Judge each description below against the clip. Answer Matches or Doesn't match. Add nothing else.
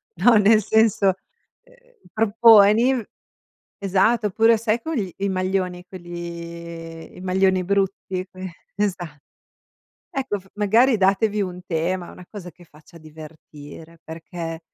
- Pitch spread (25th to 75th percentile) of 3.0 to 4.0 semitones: Matches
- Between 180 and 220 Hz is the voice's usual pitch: Matches